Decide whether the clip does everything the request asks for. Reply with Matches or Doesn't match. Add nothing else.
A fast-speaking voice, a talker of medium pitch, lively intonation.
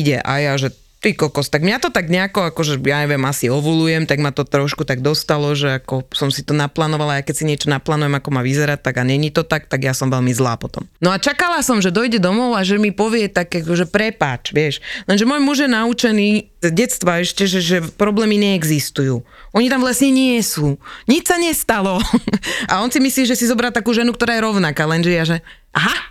Matches